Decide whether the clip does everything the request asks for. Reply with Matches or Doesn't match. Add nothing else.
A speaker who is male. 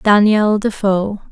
Doesn't match